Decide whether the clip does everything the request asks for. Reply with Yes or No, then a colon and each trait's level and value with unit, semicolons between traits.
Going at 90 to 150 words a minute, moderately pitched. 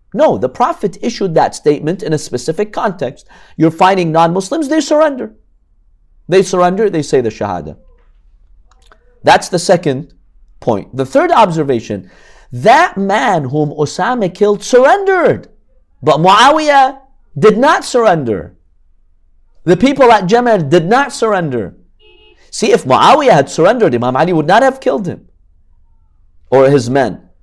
Yes: slow, 135 wpm; medium, 160 Hz